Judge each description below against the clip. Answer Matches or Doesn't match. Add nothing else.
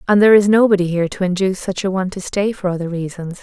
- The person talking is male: Doesn't match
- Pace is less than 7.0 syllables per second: Doesn't match